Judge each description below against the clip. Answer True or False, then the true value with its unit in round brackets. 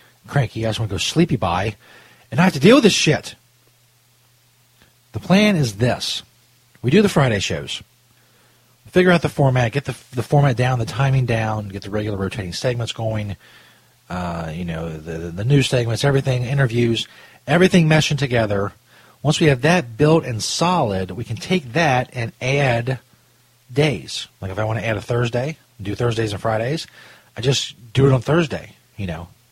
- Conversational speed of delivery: True (185 wpm)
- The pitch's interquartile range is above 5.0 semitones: False (4.3 semitones)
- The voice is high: False (120 Hz)